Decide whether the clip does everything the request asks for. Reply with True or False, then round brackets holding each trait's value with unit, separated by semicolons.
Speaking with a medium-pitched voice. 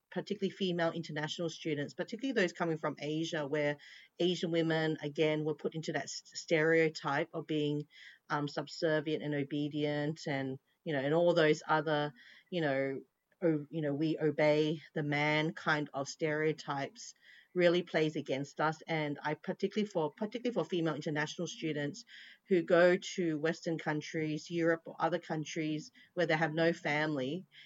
True (155 Hz)